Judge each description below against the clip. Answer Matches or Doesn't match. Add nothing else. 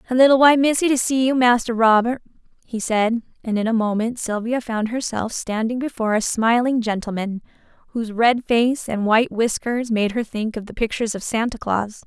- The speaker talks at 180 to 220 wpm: Matches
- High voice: Matches